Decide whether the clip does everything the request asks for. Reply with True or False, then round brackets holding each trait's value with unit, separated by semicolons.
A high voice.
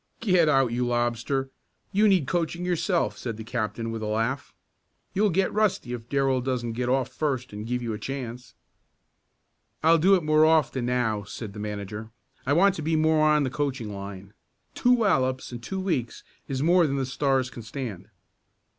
False (130 Hz)